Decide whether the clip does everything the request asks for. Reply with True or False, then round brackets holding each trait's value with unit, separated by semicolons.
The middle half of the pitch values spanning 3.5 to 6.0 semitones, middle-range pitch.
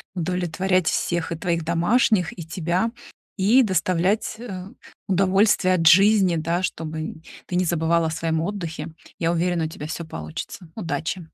False (2.5 semitones; 175 Hz)